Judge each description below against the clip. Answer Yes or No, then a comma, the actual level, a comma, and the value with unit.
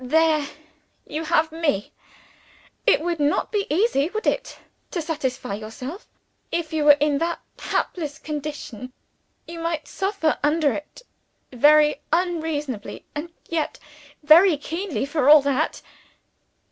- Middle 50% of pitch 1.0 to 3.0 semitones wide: Yes, narrow, 2.5 semitones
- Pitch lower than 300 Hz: No, very high, 305 Hz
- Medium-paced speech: No, slow, 125 wpm